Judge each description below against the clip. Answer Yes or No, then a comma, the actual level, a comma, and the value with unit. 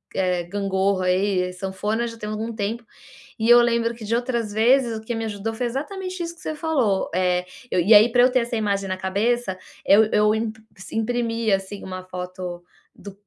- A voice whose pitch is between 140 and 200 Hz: No, high, 215 Hz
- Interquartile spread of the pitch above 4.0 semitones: No, average, 3.6 semitones